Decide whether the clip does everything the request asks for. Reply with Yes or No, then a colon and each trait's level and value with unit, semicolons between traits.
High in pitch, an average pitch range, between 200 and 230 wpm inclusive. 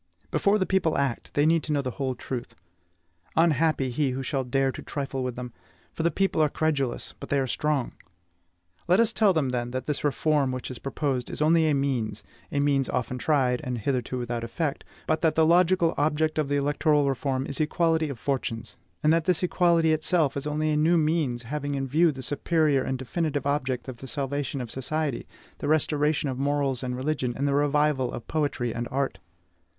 No: medium, 145 Hz; average, 3.2 semitones; fast, 205 wpm